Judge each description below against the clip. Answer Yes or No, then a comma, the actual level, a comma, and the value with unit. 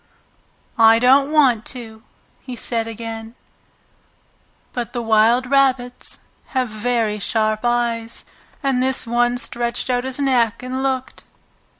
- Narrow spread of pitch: Yes, narrow, 2.2 semitones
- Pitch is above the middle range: Yes, high, 240 Hz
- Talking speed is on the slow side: Yes, slow, 120 wpm